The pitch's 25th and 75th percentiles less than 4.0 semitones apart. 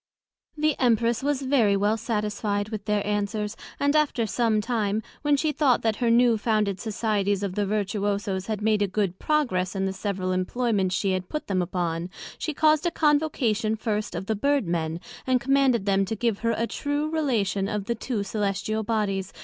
Yes: average, 3.5 semitones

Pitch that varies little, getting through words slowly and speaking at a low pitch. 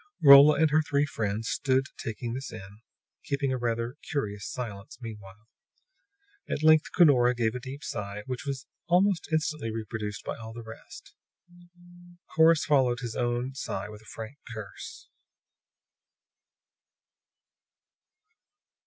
No: average, 4.5 semitones; slow, 125 wpm; low, 120 Hz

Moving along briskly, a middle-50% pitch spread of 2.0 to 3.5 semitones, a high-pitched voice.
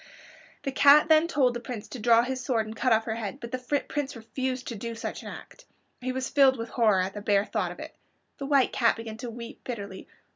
Yes: fast, 245 wpm; average, 2.9 semitones; high, 240 Hz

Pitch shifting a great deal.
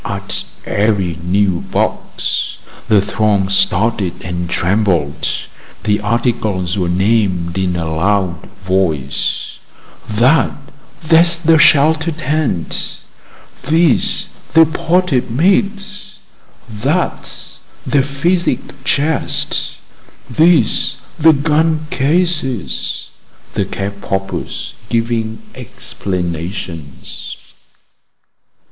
Yes: wide, 8.9 semitones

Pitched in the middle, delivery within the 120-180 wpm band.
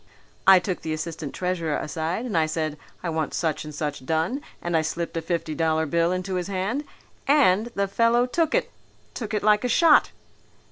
No: medium, 175 Hz; average, 195 wpm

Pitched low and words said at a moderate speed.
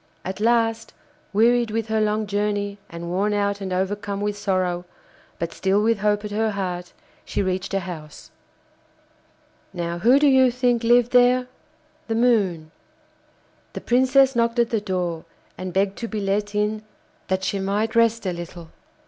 No: high, 205 Hz; average, 165 wpm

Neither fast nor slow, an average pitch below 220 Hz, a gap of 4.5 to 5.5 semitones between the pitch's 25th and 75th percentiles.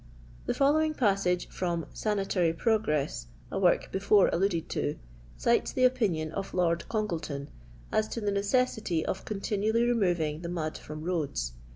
Yes: average, 155 wpm; high, 190 Hz; average, 4.9 semitones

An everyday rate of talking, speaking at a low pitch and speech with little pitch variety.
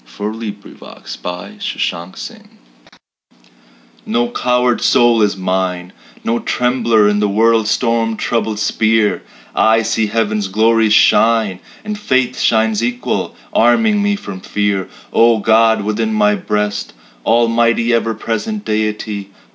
No: slow, 130 wpm; low, 110 Hz; narrow, 2.0 semitones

